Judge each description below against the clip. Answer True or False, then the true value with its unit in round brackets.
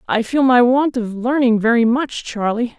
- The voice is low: False (240 Hz)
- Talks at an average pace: True (195 wpm)